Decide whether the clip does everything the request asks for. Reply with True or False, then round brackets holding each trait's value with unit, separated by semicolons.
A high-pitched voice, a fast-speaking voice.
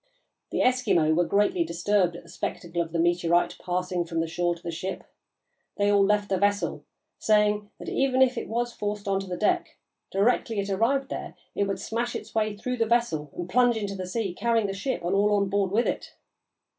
True (200 Hz; 215 wpm)